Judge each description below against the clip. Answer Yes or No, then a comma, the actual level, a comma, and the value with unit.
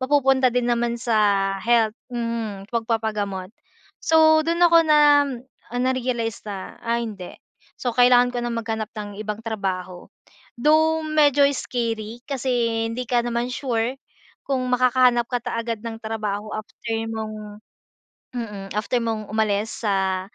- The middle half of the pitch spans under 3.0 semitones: Yes, narrow, 2.6 semitones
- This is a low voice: No, high, 230 Hz